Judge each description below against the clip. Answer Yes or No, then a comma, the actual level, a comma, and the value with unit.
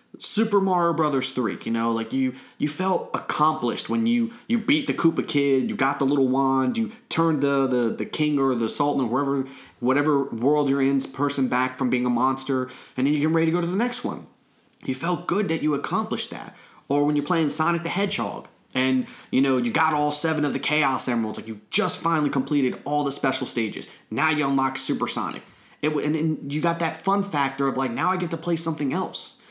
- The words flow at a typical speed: No, fast, 225 wpm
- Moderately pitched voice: Yes, medium, 145 Hz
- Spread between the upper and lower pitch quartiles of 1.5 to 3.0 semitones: No, average, 3.8 semitones